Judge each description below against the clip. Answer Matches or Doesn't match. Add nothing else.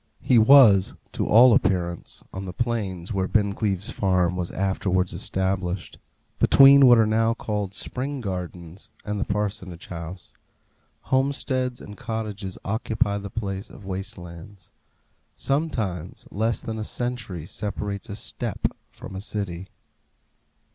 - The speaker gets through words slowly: Matches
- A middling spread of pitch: Matches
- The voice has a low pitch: Matches